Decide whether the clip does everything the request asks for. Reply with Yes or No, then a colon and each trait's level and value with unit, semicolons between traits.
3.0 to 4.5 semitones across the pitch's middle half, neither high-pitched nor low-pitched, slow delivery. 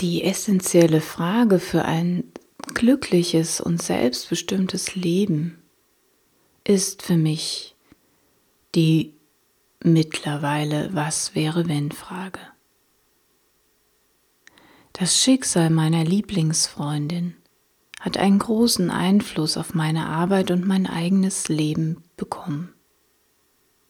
Yes: average, 3.4 semitones; medium, 170 Hz; slow, 85 wpm